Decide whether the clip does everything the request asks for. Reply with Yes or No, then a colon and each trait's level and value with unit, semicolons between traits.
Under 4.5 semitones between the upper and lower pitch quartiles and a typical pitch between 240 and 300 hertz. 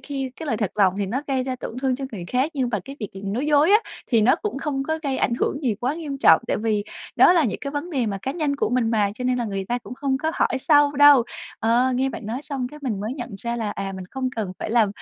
Yes: average, 4.1 semitones; very high, 255 Hz